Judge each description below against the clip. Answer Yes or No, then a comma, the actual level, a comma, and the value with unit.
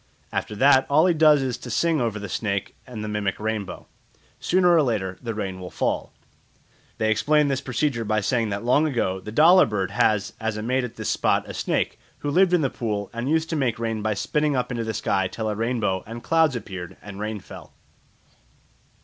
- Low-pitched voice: Yes, low, 115 Hz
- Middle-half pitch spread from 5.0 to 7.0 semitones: Yes, average, 5.3 semitones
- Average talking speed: No, fast, 215 wpm